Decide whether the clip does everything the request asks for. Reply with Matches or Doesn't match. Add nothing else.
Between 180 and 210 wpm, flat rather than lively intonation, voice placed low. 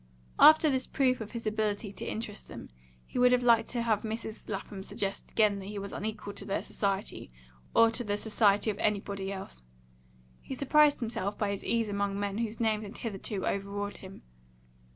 Doesn't match